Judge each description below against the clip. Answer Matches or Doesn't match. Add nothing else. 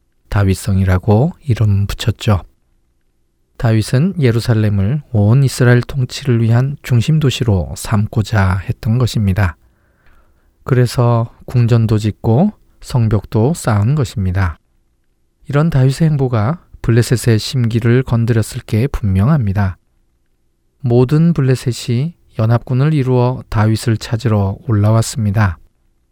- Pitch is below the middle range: Matches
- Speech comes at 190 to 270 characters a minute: Matches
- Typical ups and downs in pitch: Matches